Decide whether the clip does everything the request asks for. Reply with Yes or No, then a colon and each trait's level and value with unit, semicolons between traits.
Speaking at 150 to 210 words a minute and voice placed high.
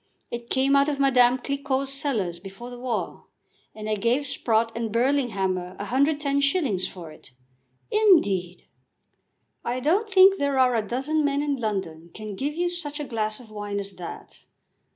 Yes: average, 160 wpm; very high, 250 Hz